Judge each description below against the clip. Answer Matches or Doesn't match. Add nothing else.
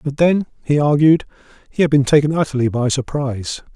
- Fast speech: Doesn't match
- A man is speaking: Matches